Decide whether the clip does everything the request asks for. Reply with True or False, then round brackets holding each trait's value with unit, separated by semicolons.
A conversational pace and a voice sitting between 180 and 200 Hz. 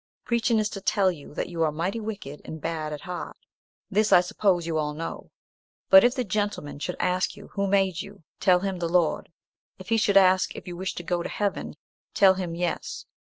False (210 wpm; 185 Hz)